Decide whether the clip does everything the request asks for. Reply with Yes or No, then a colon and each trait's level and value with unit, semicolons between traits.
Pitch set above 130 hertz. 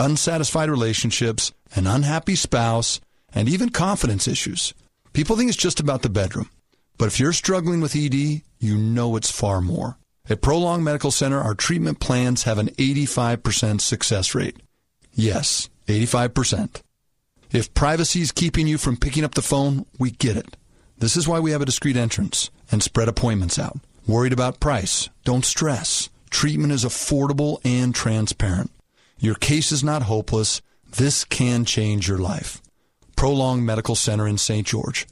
No: low, 125 Hz